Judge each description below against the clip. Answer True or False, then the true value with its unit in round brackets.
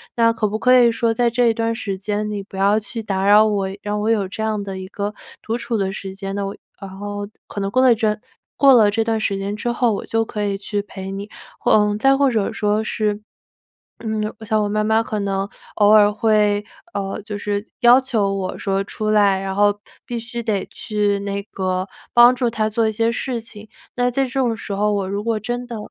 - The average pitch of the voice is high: True (210 Hz)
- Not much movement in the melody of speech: True (2.2 semitones)